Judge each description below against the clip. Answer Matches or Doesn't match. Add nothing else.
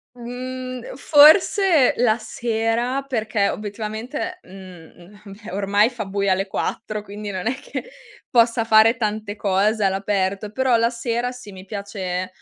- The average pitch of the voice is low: Doesn't match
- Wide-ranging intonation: Doesn't match